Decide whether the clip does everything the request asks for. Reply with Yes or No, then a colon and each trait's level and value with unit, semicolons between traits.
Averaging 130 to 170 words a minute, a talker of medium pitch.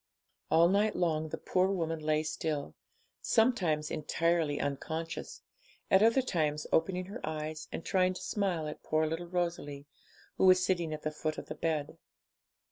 Yes: average, 160 wpm; medium, 165 Hz